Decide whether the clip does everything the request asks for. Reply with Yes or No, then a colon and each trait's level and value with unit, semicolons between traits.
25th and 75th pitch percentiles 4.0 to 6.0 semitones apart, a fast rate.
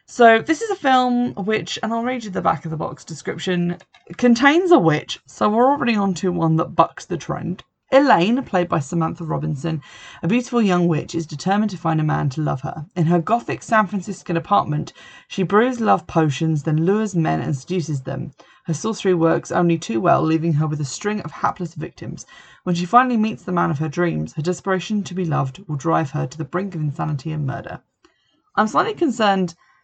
Yes: average, 4.9 semitones; fast, 210 wpm